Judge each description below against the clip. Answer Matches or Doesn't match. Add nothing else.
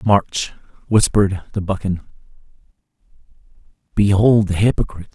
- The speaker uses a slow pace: Matches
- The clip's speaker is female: Doesn't match